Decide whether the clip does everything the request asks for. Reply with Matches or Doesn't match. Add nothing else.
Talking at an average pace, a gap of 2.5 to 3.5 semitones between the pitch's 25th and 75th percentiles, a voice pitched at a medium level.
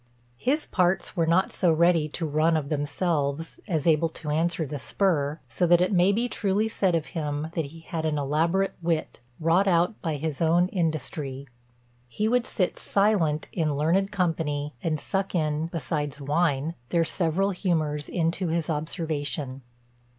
Matches